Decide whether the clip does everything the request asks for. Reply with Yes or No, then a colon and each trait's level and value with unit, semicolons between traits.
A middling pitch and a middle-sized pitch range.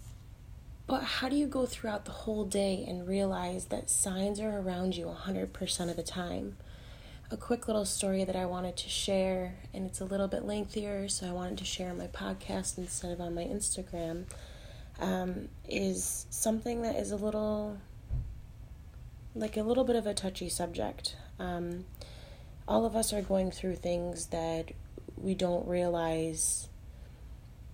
No: medium, 180 Hz; wide, 6.0 semitones